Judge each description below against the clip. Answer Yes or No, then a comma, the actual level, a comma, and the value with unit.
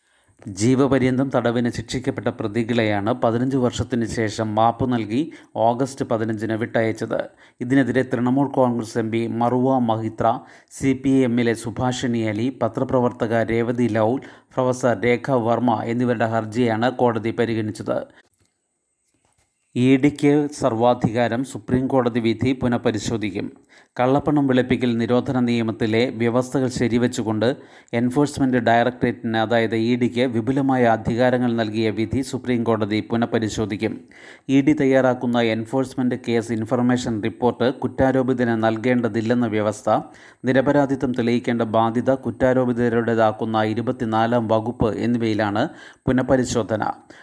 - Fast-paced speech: No, average, 95 wpm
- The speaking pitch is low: Yes, low, 120 Hz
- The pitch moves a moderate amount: No, narrow, 2.1 semitones